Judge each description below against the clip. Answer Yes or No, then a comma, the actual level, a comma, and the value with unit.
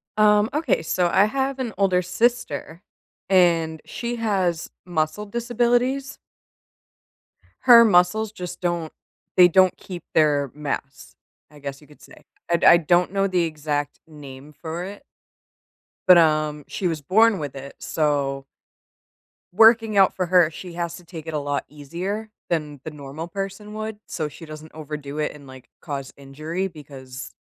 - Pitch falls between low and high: Yes, medium, 170 Hz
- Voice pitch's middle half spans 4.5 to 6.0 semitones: Yes, average, 4.9 semitones